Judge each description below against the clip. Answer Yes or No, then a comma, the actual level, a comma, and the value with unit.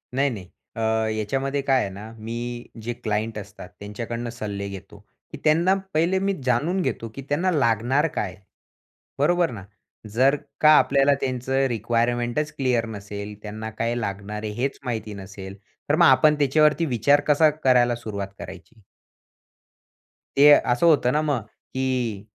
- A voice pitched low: Yes, low, 120 Hz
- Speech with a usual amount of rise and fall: Yes, average, 4.8 semitones